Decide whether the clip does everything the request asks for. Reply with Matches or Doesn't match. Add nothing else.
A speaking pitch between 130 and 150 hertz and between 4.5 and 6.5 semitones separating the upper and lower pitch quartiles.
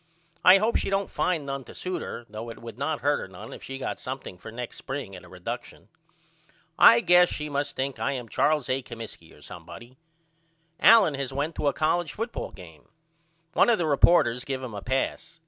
Matches